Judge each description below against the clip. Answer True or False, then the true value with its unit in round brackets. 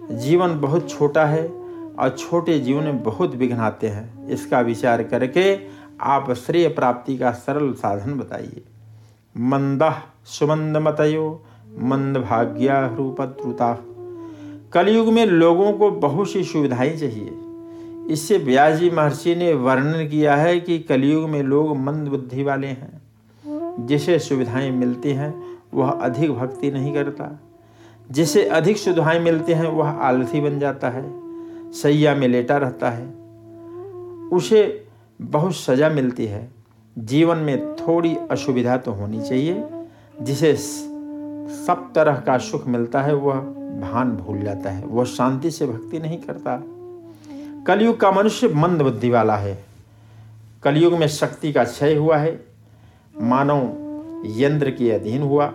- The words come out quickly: False (135 wpm)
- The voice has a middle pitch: True (145 Hz)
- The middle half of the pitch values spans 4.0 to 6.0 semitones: True (5.4 semitones)